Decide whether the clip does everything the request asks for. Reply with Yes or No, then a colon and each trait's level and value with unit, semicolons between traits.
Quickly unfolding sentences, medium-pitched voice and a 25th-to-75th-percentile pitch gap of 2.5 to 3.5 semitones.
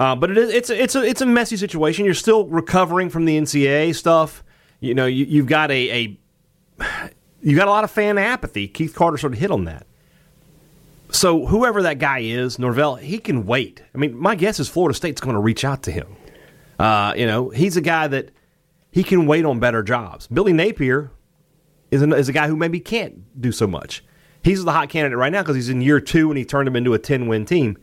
No: fast, 235 wpm; medium, 155 Hz; average, 5.0 semitones